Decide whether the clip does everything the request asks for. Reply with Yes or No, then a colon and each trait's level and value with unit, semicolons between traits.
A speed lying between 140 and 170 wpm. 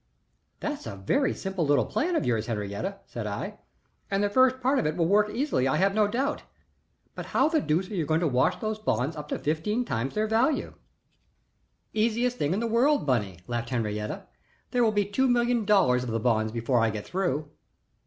No: fast, 205 wpm